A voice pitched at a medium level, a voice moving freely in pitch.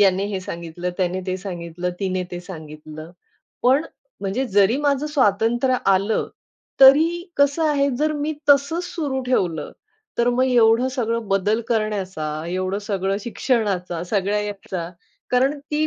No: high, 210 Hz; wide, 6.2 semitones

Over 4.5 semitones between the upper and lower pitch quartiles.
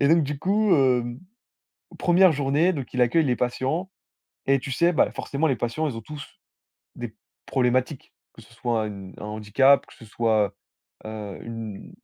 Yes: average, 4.9 semitones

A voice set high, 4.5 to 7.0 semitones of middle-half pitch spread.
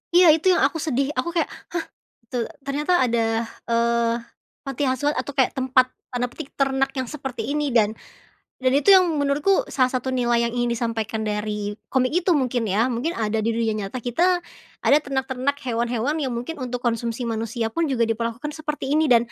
No: very high, 255 Hz; average, 3.5 semitones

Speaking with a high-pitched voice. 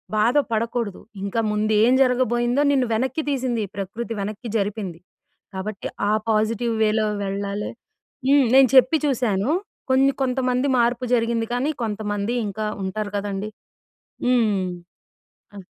Yes: high, 230 Hz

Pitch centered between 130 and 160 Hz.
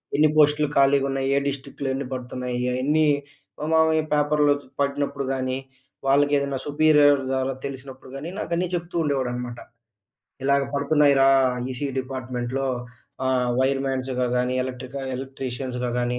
Yes: low, 135 Hz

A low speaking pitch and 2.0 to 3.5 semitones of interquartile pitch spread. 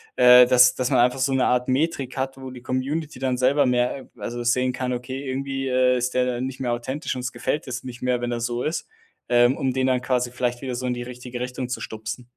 No: low, 125 Hz; narrow, 1.2 semitones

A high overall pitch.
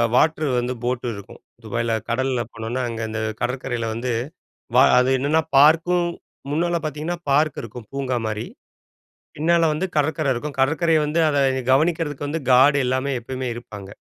No: low, 135 Hz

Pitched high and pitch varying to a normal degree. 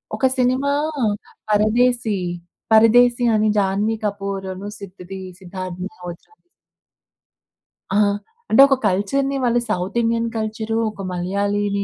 Yes: high, 210 Hz; average, 3.3 semitones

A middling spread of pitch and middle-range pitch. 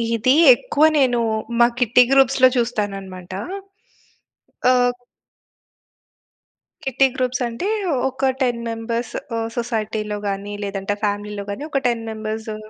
No: average, 3.1 semitones; high, 230 Hz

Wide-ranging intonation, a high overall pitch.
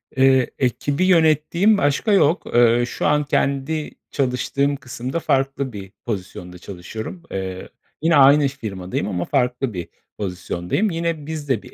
No: wide, 5.9 semitones; low, 135 Hz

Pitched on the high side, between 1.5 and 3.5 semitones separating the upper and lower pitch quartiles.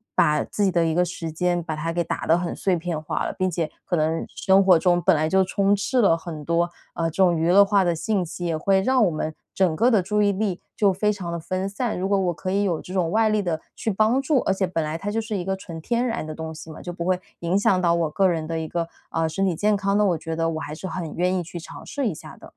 No: medium, 180 Hz; average, 3.2 semitones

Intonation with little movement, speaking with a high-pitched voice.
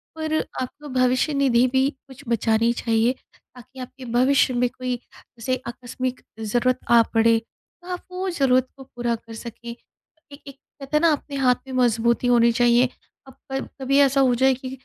Yes: narrow, 2.2 semitones; very high, 255 Hz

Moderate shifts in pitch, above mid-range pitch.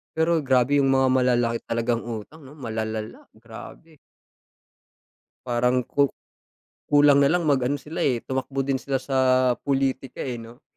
No: average, 3.1 semitones; low, 130 Hz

